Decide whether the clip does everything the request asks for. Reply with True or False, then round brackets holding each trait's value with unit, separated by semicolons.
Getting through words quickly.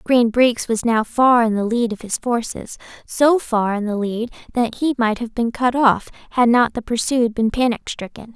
True (215 wpm)